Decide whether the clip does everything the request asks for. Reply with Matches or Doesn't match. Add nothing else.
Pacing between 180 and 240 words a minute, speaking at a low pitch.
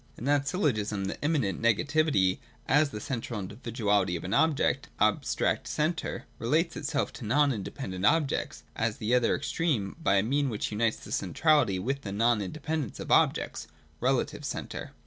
Doesn't match